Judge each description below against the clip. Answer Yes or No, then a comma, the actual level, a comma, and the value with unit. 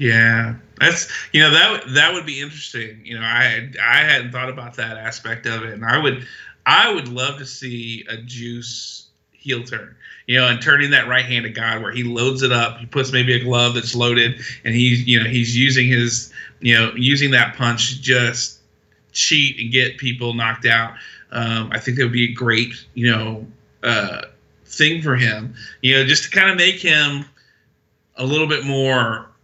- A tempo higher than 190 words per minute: Yes, average, 200 wpm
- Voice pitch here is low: Yes, low, 120 Hz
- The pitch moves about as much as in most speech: No, narrow, 2.1 semitones